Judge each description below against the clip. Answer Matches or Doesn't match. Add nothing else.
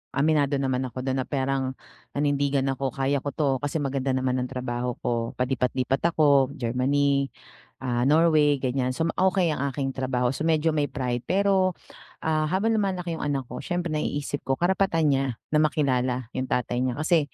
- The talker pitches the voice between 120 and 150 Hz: Matches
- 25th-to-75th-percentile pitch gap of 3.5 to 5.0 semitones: Doesn't match